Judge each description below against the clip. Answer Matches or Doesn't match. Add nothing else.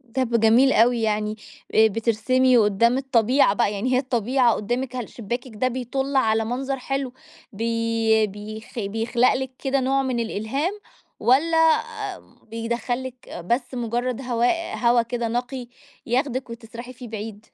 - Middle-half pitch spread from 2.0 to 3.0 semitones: Matches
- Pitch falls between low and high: Doesn't match